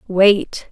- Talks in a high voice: Yes, high, 195 Hz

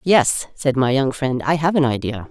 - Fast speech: Yes, fast, 235 wpm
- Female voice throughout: Yes, female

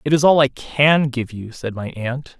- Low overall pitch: Yes, low, 130 Hz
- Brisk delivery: Yes, fast, 250 wpm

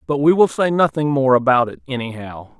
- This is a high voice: No, low, 135 Hz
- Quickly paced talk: Yes, fast, 210 wpm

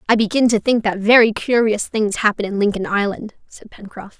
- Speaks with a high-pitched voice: Yes, high, 215 Hz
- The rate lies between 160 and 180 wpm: No, average, 200 wpm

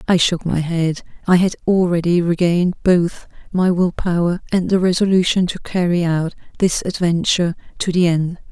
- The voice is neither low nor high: Yes, medium, 175 Hz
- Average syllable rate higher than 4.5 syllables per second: Yes, 5.0 syllables/s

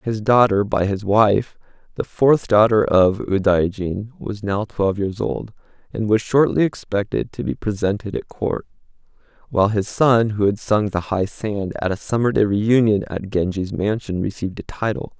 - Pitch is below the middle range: Yes, low, 105 Hz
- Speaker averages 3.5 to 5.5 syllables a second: Yes, 4.7 syllables/s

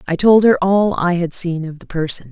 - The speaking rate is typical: No, fast, 260 wpm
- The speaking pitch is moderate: Yes, medium, 175 Hz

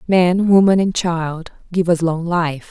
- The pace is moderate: Yes, average, 180 wpm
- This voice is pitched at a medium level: Yes, medium, 175 Hz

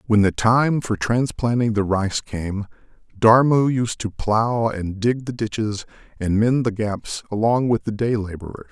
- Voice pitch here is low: Yes, low, 110 Hz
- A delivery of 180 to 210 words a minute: No, average, 170 wpm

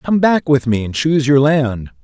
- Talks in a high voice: No, medium, 145 Hz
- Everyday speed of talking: No, fast, 235 wpm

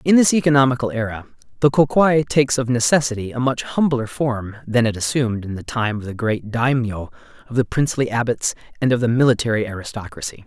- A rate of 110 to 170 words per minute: No, average, 190 wpm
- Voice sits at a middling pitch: No, low, 120 Hz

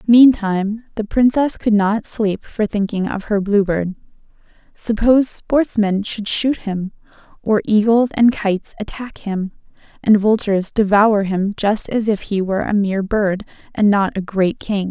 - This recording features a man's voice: No, female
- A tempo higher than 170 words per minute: No, average, 160 wpm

